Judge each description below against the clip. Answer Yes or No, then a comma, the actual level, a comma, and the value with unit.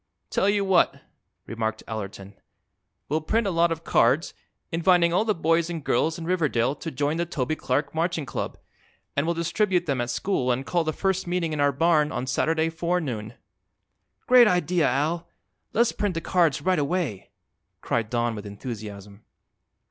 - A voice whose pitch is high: No, medium, 160 Hz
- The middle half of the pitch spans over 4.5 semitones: Yes, wide, 5.4 semitones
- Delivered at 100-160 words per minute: No, average, 170 wpm